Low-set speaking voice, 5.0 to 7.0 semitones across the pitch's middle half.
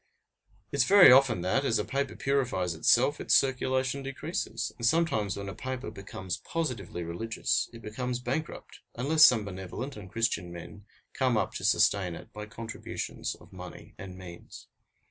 Yes: low, 115 Hz; average, 5.3 semitones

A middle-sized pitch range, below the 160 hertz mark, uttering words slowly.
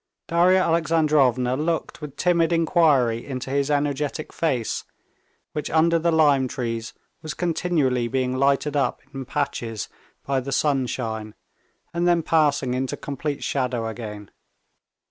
Yes: average, 4.1 semitones; medium, 140 Hz; slow, 125 wpm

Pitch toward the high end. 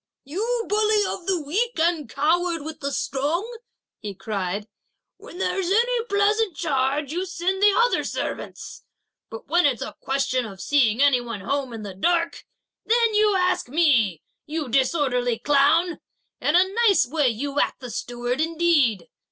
Yes: very high, 300 Hz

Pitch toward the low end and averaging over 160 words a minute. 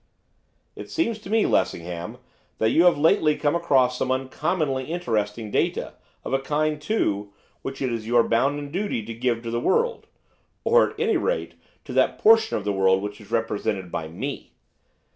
Yes: low, 130 Hz; average, 180 wpm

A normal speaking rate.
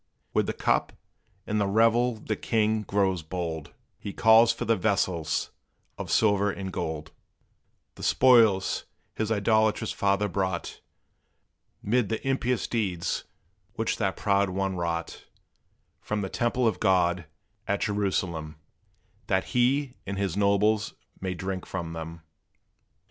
No: slow, 130 wpm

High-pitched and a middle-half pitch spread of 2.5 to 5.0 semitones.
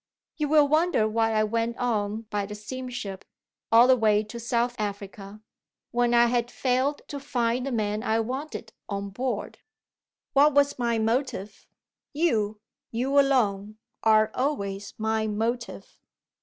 Yes: high, 230 Hz; average, 3.3 semitones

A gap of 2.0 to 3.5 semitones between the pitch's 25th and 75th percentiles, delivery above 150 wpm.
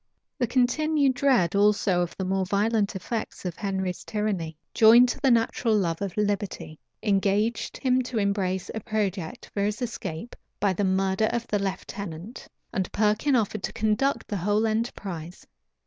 Yes: average, 3.1 semitones; average, 160 wpm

